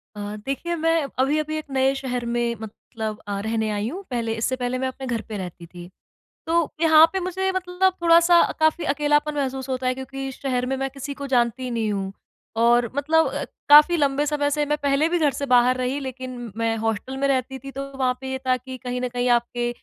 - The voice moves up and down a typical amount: Yes, average, 3.6 semitones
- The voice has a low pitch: No, very high, 265 Hz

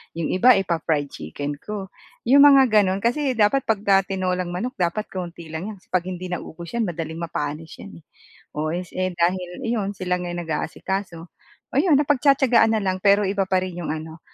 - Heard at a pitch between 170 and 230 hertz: Yes, medium, 185 Hz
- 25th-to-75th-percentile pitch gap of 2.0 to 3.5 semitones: No, average, 4.0 semitones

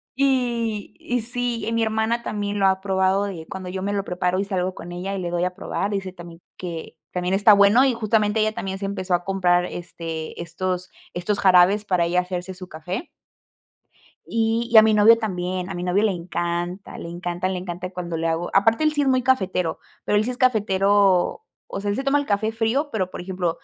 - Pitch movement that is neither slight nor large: Yes, average, 3.5 semitones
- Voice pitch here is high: Yes, high, 195 Hz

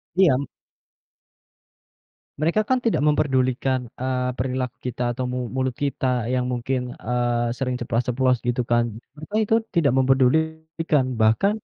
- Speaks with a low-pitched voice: Yes, low, 130 Hz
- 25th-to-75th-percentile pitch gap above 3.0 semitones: No, average, 2.7 semitones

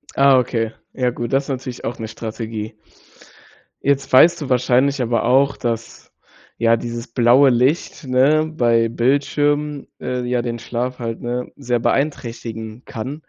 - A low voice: Yes, low, 125 Hz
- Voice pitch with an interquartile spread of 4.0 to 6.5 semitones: No, average, 2.8 semitones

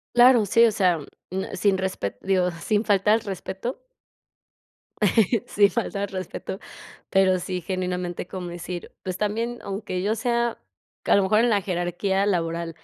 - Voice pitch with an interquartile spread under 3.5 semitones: Yes, average, 2.8 semitones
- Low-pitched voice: No, high, 190 Hz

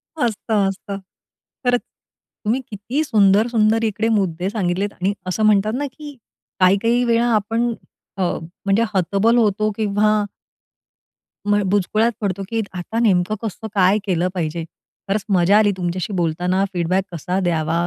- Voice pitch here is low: No, high, 205 Hz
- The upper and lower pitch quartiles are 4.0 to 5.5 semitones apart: No, average, 3.4 semitones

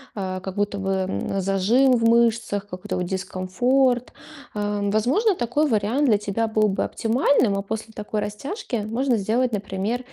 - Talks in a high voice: Yes, high, 215 Hz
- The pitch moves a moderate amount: Yes, average, 3.5 semitones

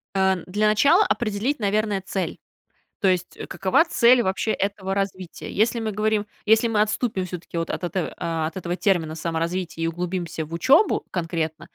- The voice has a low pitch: No, high, 190 Hz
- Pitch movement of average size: Yes, average, 3.7 semitones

